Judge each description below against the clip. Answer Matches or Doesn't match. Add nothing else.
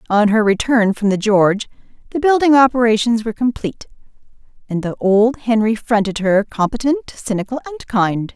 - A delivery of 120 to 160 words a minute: Matches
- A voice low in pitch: Doesn't match